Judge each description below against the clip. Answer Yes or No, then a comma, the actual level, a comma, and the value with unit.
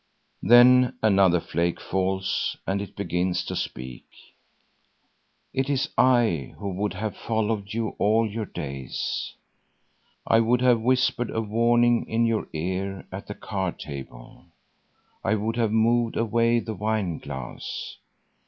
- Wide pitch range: No, average, 3.7 semitones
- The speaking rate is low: Yes, slow, 130 wpm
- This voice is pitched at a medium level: No, low, 110 Hz